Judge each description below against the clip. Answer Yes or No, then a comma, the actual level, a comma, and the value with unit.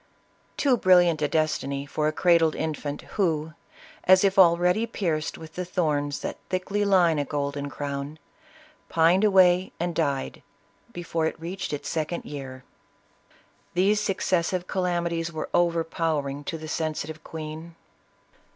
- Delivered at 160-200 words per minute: No, slow, 135 wpm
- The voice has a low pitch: No, medium, 165 Hz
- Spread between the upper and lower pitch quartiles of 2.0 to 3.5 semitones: Yes, average, 2.9 semitones